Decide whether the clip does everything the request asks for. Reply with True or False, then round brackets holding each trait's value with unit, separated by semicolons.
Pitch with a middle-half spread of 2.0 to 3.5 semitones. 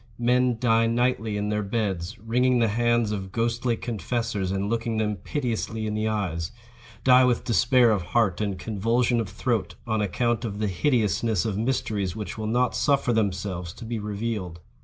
True (2.7 semitones)